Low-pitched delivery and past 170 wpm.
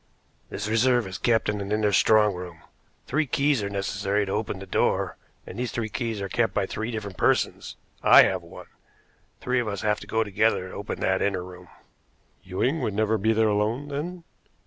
Yes: low, 105 Hz; average, 200 wpm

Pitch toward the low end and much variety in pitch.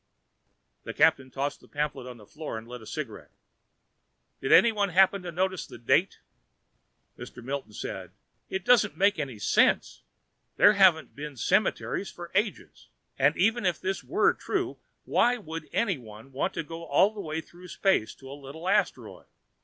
No: medium, 160 Hz; wide, 6.1 semitones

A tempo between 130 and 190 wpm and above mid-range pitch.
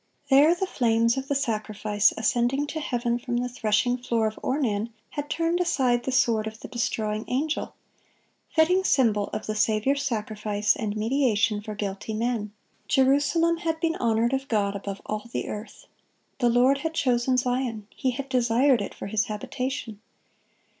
Yes: average, 160 wpm; high, 240 Hz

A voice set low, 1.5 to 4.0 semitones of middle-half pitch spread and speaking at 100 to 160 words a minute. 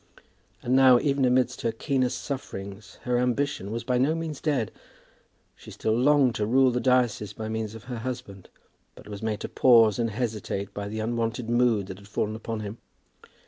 No: low, 115 Hz; average, 3.0 semitones; average, 185 wpm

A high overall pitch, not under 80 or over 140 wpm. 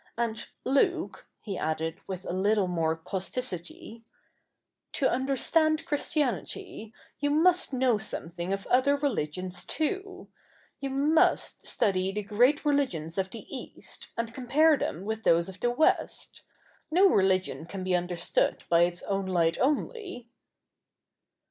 Yes: high, 220 Hz; slow, 135 wpm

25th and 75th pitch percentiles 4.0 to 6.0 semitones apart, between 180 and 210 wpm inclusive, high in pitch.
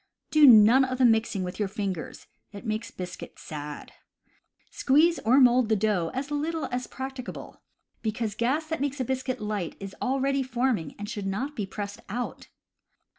Yes: average, 4.4 semitones; average, 185 wpm; high, 235 Hz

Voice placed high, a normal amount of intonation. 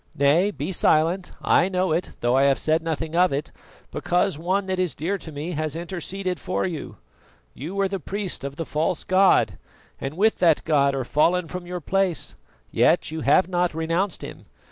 No: medium, 170 Hz; average, 3.2 semitones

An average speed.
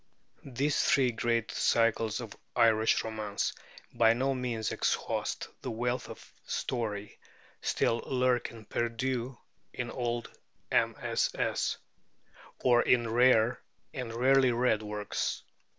No: slow, 105 wpm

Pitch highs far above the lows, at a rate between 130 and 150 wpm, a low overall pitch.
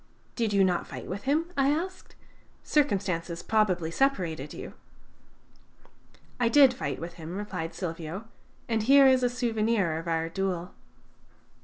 No: wide, 6.9 semitones; average, 140 wpm; high, 200 Hz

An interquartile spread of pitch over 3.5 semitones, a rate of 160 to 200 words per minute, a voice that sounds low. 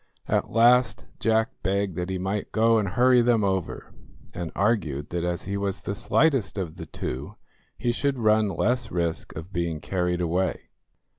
Yes: average, 4.5 semitones; average, 170 wpm; low, 100 Hz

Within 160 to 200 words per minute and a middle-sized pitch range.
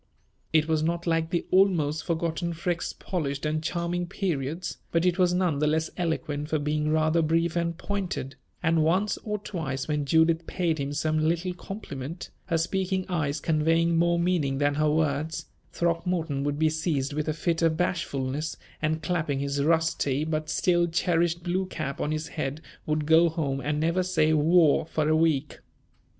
No: average, 175 wpm; narrow, 2.2 semitones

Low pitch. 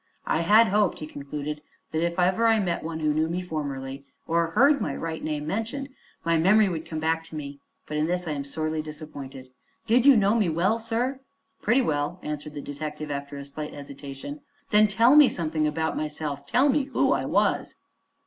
No: medium, 160 Hz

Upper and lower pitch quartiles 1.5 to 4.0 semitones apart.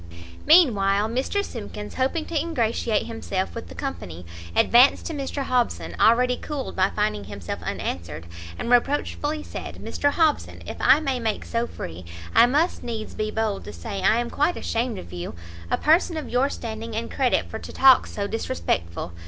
No: wide, 5.4 semitones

